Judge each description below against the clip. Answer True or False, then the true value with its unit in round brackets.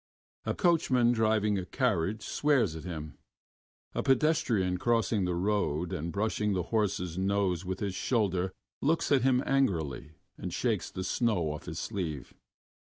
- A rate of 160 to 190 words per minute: False (150 wpm)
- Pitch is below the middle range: True (100 Hz)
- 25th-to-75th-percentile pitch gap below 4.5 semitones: False (5.0 semitones)